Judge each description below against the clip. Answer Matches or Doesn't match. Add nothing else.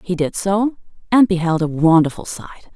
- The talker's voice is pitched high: Doesn't match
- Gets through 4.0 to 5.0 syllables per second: Doesn't match